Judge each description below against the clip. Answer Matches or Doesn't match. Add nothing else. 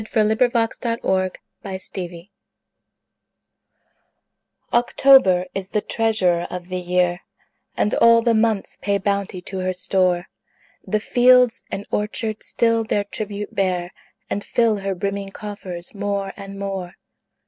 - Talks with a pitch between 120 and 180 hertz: Doesn't match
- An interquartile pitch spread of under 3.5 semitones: Matches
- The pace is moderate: Doesn't match